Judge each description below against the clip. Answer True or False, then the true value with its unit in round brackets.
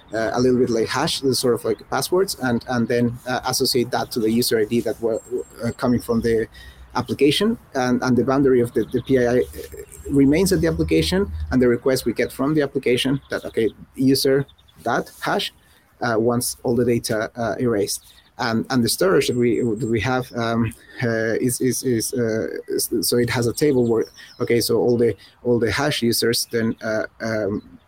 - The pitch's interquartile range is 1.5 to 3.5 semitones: True (2.6 semitones)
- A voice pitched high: False (120 Hz)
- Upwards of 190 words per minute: True (200 wpm)